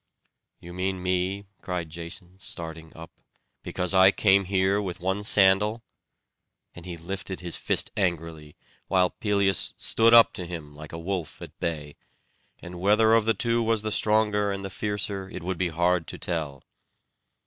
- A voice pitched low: Yes, very low, 95 Hz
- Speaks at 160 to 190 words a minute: Yes, average, 165 wpm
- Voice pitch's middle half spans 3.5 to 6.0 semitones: No, average, 3.0 semitones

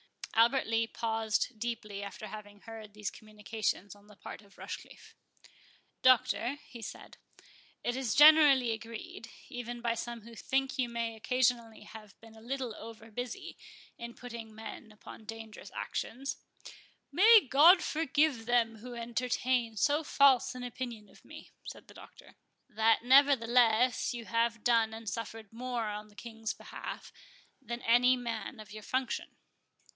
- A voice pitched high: Yes, high, 230 Hz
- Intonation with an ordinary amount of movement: No, narrow, 2.2 semitones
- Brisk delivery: No, average, 150 wpm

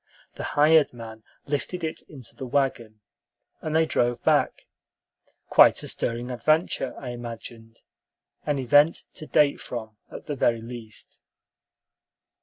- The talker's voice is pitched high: No, low, 125 Hz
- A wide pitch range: No, average, 4.2 semitones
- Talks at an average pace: No, slow, 130 wpm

